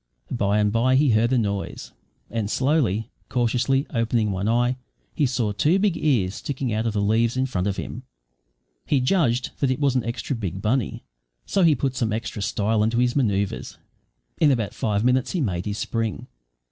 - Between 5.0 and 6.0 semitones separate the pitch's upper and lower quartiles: No, average, 3.7 semitones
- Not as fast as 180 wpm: No, average, 190 wpm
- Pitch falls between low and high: No, low, 115 Hz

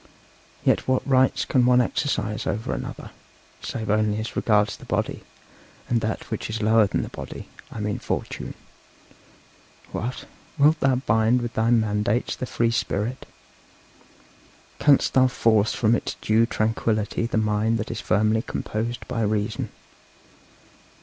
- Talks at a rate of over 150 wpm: No, average, 145 wpm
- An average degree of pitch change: No, narrow, 2.1 semitones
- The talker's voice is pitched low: Yes, low, 110 Hz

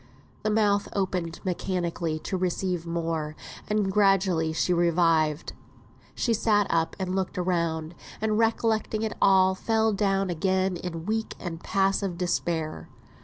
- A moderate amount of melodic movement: Yes, average, 3.1 semitones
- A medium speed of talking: No, slow, 125 wpm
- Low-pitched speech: No, medium, 185 Hz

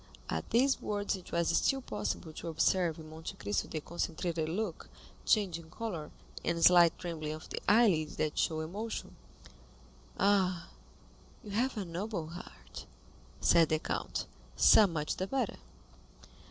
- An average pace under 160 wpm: Yes, average, 140 wpm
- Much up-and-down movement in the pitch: No, average, 4.3 semitones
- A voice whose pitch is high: No, medium, 170 Hz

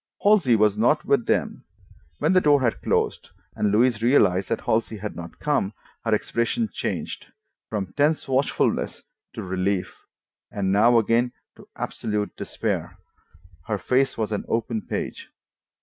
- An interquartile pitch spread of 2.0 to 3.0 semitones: No, average, 4.1 semitones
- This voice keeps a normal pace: Yes, average, 145 wpm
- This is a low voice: Yes, low, 115 Hz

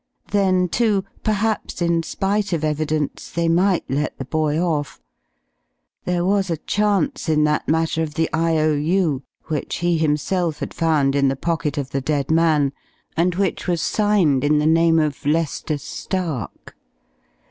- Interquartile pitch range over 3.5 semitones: No, average, 3.2 semitones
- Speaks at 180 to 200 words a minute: No, average, 155 wpm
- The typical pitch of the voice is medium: Yes, medium, 160 Hz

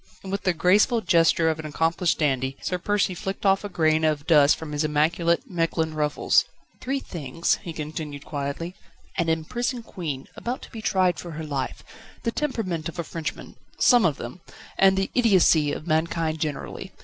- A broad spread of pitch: No, average, 3.8 semitones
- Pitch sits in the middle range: Yes, medium, 165 Hz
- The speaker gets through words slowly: No, average, 180 wpm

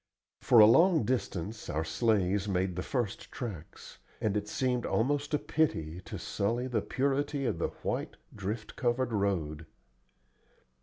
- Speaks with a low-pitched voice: Yes, low, 110 Hz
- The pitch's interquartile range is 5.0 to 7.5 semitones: Yes, wide, 5.4 semitones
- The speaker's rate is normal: Yes, average, 145 wpm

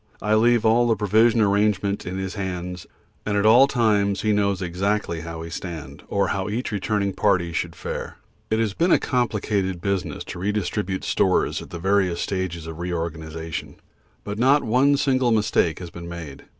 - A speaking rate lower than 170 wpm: No, average, 175 wpm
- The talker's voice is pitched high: No, low, 100 Hz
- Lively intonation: No, average, 3.7 semitones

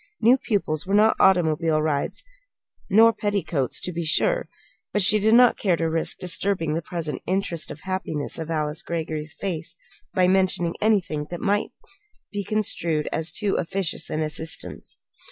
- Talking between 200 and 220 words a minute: No, average, 155 wpm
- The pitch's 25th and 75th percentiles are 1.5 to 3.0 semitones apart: No, average, 4.1 semitones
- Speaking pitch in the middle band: Yes, medium, 175 Hz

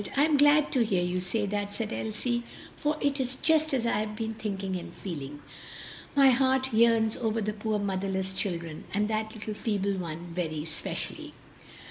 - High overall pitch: Yes, high, 215 Hz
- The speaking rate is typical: Yes, average, 180 wpm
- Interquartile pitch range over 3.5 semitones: Yes, average, 4.0 semitones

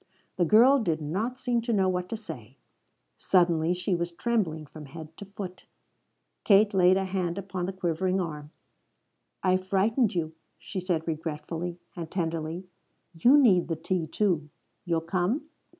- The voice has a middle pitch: Yes, medium, 180 Hz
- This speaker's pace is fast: No, average, 155 wpm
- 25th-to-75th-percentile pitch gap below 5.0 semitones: Yes, average, 3.3 semitones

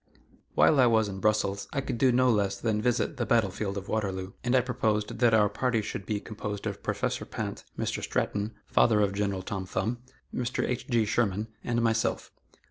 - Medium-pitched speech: No, low, 110 Hz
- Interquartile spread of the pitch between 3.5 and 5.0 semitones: No, average, 3.1 semitones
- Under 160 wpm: No, average, 200 wpm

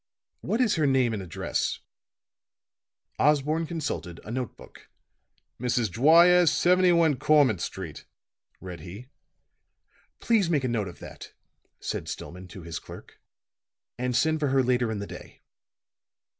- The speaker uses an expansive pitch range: Yes, wide, 7.8 semitones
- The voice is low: Yes, low, 130 Hz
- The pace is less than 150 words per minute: Yes, slow, 135 wpm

